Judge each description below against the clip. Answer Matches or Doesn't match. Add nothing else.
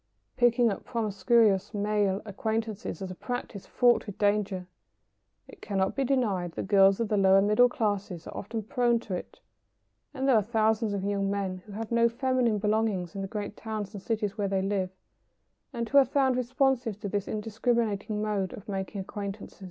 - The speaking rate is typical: Matches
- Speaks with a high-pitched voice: Matches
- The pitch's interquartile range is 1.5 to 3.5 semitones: Matches